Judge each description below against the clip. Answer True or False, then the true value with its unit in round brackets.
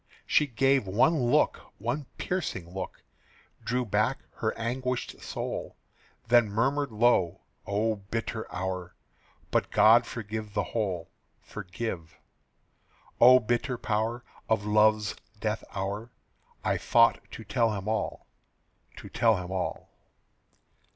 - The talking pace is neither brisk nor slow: False (115 wpm)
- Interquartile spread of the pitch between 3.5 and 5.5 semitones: False (3.1 semitones)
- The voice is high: False (110 Hz)